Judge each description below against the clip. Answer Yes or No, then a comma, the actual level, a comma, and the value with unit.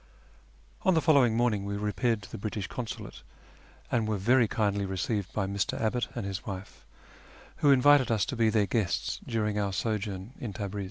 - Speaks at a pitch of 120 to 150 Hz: No, low, 105 Hz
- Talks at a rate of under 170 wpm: No, average, 180 wpm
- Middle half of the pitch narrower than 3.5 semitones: Yes, average, 3.0 semitones